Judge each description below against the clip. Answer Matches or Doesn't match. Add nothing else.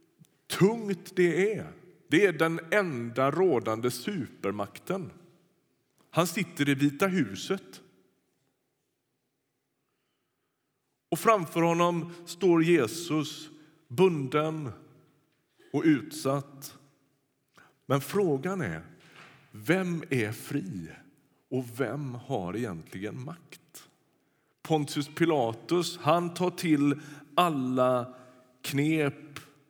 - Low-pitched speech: Doesn't match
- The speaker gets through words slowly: Matches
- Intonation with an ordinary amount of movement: Matches